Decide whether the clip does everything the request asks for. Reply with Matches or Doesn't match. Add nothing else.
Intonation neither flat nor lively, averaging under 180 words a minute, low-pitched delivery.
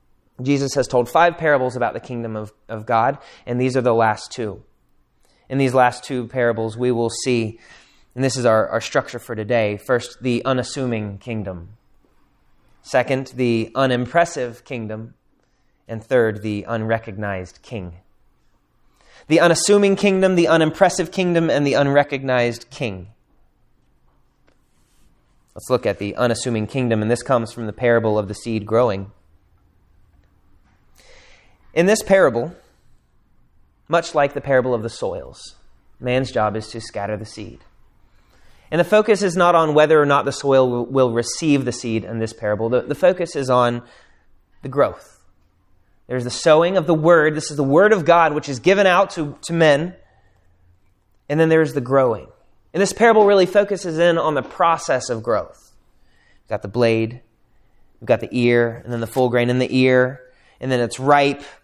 Matches